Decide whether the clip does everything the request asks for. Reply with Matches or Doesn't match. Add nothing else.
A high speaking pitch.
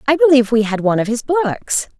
Matches